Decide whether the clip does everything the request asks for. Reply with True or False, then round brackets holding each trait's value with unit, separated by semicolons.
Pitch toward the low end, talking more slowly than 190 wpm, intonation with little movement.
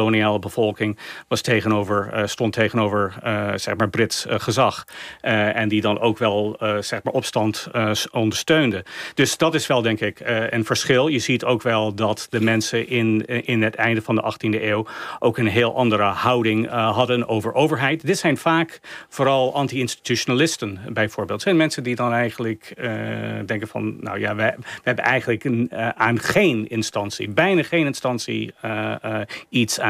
True (115 Hz; 180 wpm; 2.3 semitones)